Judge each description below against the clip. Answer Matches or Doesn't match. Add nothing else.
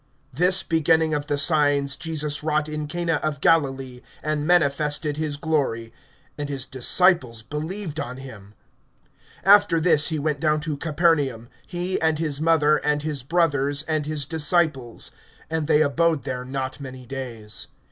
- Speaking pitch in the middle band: Matches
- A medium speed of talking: Matches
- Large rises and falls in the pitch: Doesn't match